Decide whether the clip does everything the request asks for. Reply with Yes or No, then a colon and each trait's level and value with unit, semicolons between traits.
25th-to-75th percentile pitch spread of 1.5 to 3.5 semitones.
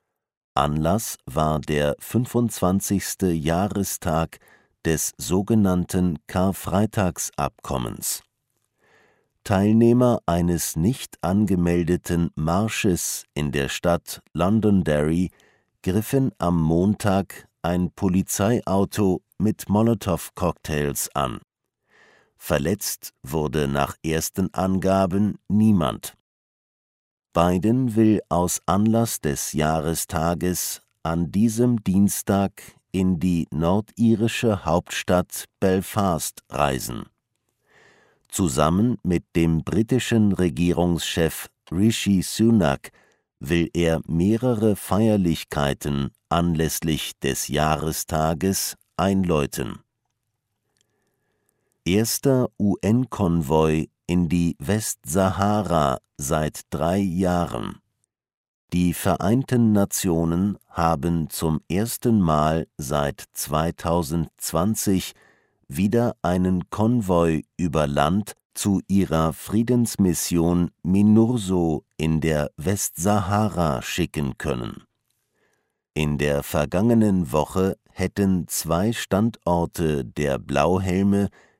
No: average, 4.3 semitones